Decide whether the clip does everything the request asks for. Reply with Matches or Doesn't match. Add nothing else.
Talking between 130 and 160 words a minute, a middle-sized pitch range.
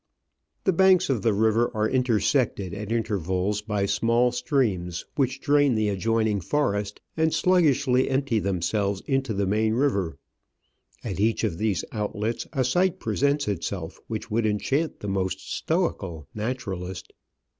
Matches